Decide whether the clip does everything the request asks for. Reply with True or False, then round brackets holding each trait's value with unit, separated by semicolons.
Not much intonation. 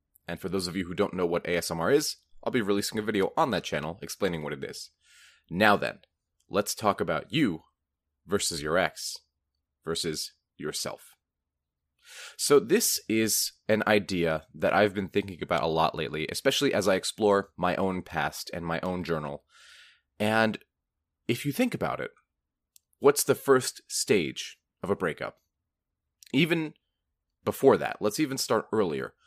False (4.6 semitones)